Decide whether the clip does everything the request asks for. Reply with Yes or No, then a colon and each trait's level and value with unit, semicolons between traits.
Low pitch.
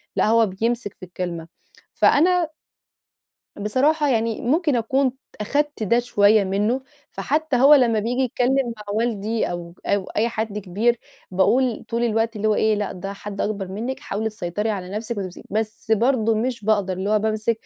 No: high, 220 Hz